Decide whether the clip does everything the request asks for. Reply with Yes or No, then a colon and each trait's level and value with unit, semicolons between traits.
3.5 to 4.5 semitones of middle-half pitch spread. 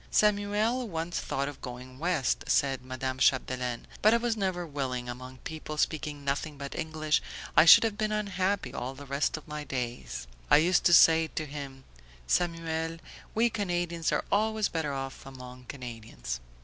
No: average, 5.1 semitones